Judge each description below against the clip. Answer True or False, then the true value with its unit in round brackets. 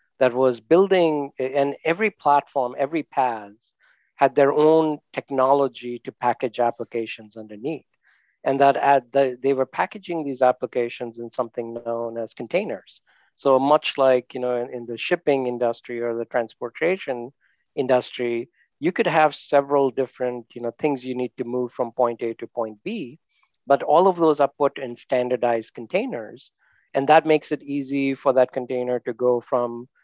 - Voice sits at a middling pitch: False (130 Hz)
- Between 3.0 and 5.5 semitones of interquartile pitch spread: False (2.6 semitones)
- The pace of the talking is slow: False (160 wpm)